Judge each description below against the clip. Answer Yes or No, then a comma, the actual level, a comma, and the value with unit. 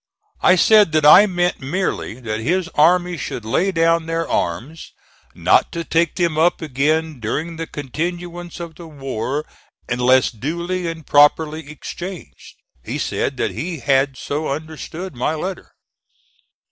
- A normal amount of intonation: Yes, average, 3.6 semitones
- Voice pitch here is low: No, medium, 160 Hz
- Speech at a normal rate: Yes, average, 145 wpm